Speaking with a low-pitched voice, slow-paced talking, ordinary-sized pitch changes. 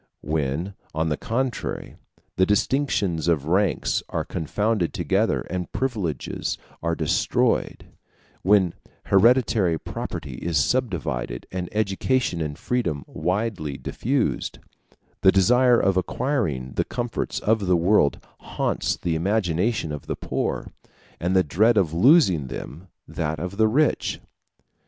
No: very low, 95 Hz; slow, 125 wpm; wide, 5.7 semitones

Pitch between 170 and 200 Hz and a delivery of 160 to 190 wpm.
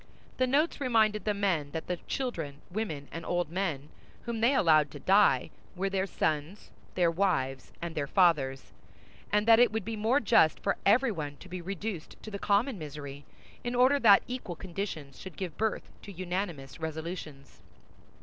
Yes: medium, 185 Hz; average, 170 wpm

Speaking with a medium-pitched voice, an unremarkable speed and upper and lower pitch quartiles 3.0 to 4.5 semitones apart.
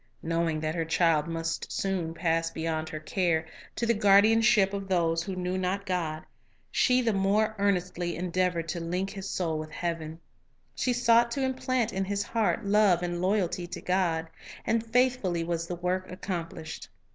Yes: medium, 180 Hz; average, 180 wpm; average, 3.4 semitones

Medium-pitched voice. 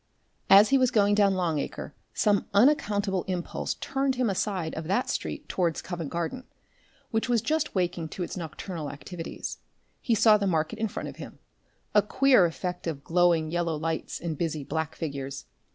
Yes: medium, 180 Hz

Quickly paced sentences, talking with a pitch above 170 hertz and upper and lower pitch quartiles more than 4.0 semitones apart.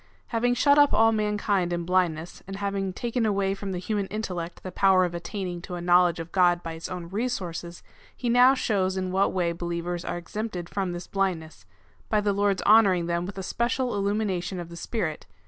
No: fast, 210 wpm; high, 190 Hz; average, 3.1 semitones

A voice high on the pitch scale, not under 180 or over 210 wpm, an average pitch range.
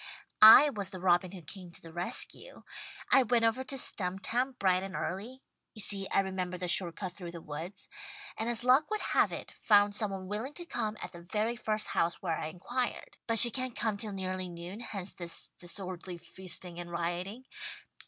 Yes: high, 195 Hz; average, 200 wpm; average, 4.1 semitones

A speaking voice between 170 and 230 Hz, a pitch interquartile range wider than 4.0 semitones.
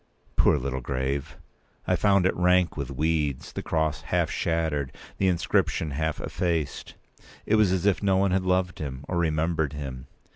No: very low, 80 Hz; average, 4.4 semitones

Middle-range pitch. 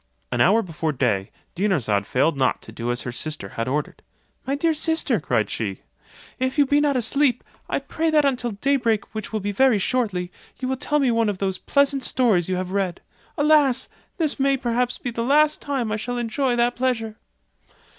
No: high, 230 Hz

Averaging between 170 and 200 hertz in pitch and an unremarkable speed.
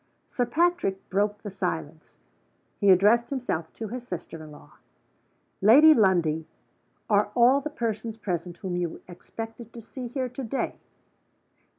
No: high, 210 Hz; average, 145 wpm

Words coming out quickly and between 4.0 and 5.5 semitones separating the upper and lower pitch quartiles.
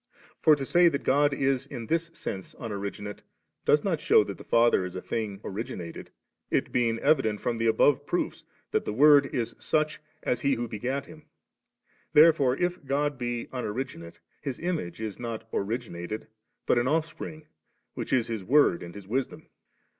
No: average, 175 wpm; average, 4.9 semitones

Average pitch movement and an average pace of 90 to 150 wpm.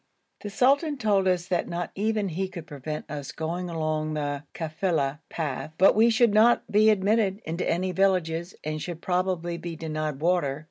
No: average, 4.0 semitones; average, 175 wpm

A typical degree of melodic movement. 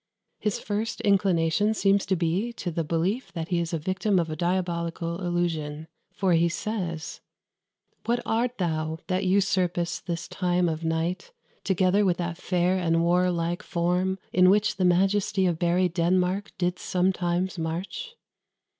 No: narrow, 2.2 semitones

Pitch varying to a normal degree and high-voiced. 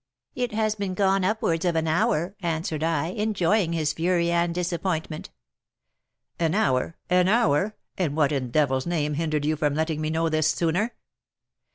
No: average, 3.3 semitones; medium, 165 Hz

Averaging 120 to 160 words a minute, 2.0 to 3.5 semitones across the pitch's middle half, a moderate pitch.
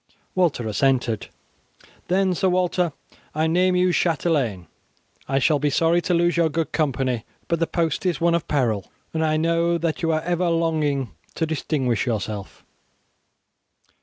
No: average, 155 wpm; average, 4.0 semitones; medium, 160 Hz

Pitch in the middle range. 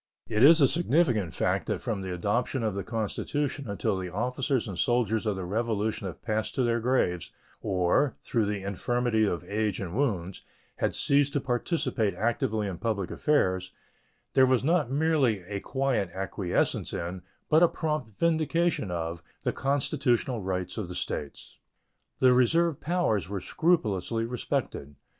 No: low, 110 Hz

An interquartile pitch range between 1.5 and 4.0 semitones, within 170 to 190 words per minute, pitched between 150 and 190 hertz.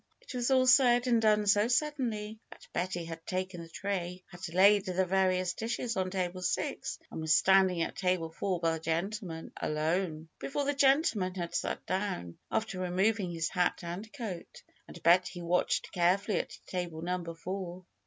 Yes: average, 3.4 semitones; average, 175 wpm; medium, 185 Hz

